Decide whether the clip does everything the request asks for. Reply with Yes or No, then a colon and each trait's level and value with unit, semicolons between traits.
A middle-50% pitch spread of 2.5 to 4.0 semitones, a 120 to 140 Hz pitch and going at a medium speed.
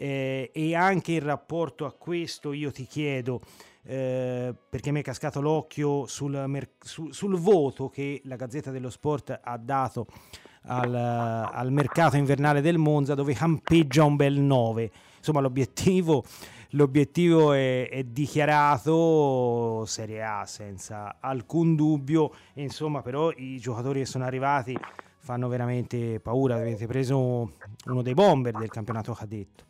Yes: average, 3.4 semitones; low, 135 Hz; average, 135 wpm